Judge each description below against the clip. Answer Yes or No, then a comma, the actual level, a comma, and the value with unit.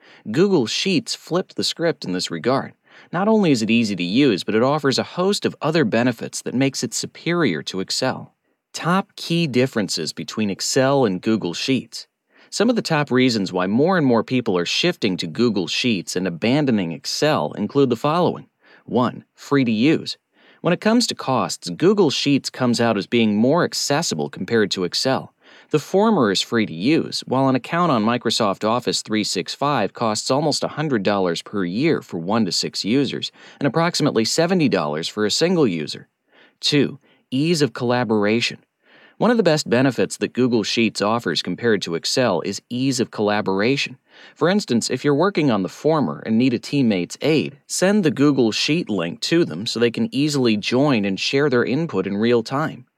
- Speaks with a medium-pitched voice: No, low, 125 Hz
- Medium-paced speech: Yes, average, 180 wpm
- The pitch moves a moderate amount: No, wide, 5.8 semitones